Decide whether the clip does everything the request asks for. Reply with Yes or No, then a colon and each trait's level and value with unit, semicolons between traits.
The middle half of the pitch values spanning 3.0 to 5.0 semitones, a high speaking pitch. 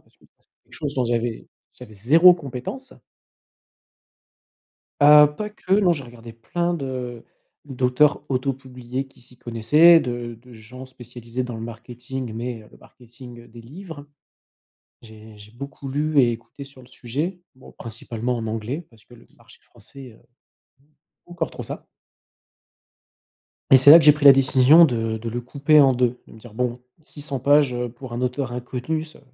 No: average, 3.4 semitones; low, 125 Hz